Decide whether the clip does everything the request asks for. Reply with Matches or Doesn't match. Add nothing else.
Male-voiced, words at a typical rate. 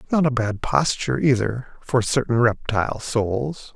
Matches